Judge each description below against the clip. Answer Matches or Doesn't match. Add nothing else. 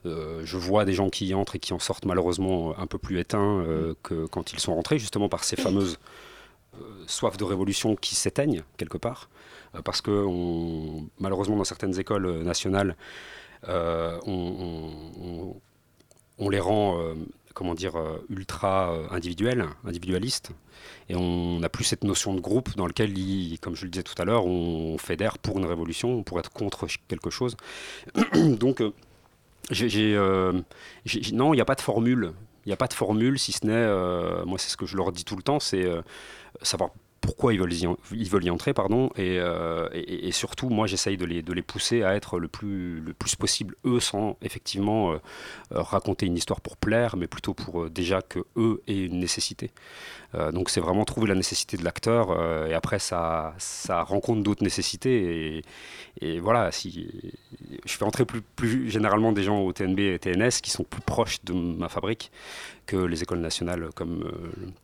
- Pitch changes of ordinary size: Matches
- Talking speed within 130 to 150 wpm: Doesn't match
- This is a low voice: Matches